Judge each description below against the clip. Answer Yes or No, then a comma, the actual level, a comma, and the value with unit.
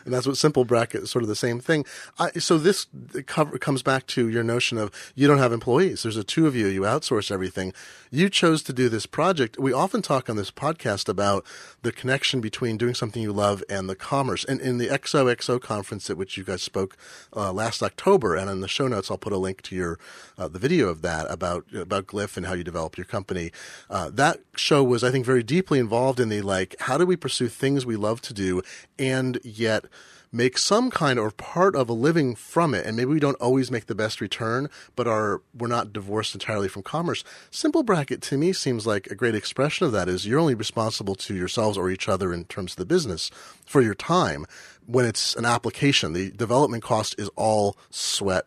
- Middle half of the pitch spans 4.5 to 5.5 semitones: Yes, average, 4.8 semitones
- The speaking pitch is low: Yes, low, 120 Hz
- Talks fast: Yes, fast, 230 wpm